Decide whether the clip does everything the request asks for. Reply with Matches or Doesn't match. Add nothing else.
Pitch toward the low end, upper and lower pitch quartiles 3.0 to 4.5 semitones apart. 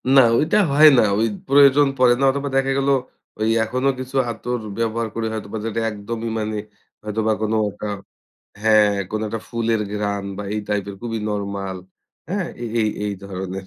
Matches